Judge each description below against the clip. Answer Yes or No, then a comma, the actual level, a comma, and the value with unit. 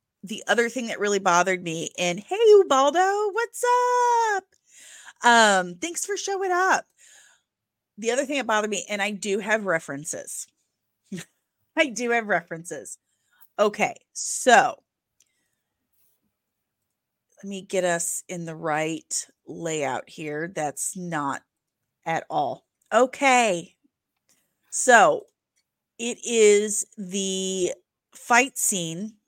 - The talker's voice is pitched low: No, high, 210 Hz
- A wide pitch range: Yes, wide, 7.7 semitones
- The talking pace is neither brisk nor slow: No, slow, 110 wpm